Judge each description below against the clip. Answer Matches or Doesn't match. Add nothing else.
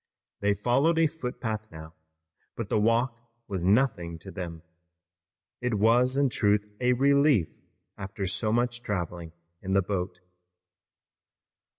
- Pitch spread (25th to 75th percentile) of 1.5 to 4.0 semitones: Doesn't match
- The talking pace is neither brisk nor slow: Doesn't match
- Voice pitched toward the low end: Matches